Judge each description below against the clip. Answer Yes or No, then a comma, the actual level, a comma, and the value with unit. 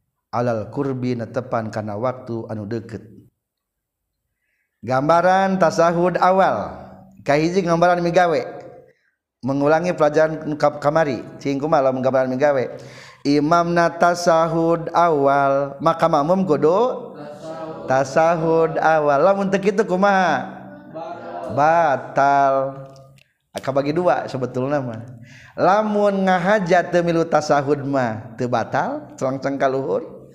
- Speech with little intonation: No, average, 4.3 semitones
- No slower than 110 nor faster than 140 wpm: No, average, 95 wpm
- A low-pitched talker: No, medium, 145 Hz